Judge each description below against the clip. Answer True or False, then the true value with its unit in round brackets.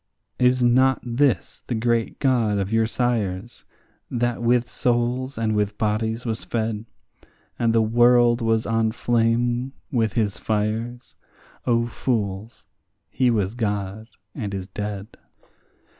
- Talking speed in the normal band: False (130 wpm)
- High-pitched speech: False (115 Hz)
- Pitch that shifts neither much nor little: False (2.1 semitones)